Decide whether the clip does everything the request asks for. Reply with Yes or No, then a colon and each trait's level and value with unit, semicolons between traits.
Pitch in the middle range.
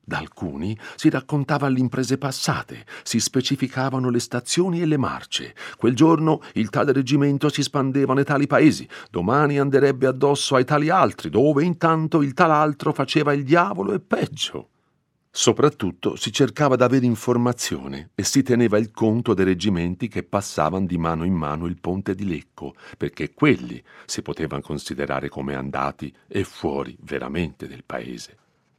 No: low, 130 Hz